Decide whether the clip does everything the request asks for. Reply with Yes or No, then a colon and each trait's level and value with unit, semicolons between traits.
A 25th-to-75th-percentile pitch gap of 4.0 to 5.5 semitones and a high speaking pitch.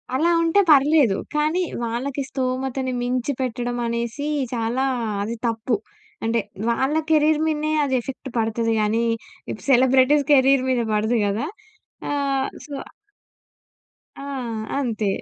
No: average, 3.3 semitones; very high, 260 Hz